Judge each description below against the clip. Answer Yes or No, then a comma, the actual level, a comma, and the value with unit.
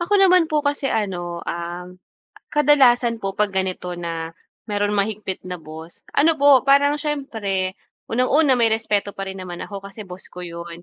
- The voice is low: No, high, 205 Hz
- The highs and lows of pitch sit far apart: Yes, wide, 7.3 semitones